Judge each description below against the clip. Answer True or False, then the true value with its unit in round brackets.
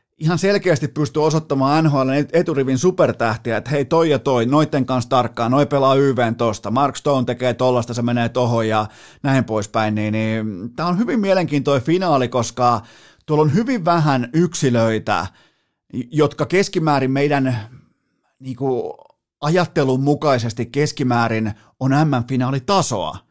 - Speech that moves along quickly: False (135 wpm)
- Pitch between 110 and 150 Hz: True (135 Hz)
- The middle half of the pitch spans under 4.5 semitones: True (4.1 semitones)